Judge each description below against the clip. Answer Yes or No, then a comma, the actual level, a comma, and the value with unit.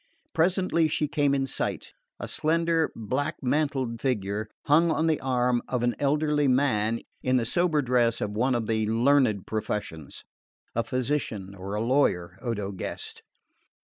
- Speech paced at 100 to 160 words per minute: Yes, average, 150 wpm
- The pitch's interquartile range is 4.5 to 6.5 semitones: Yes, average, 5.1 semitones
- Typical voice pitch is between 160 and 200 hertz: No, low, 125 Hz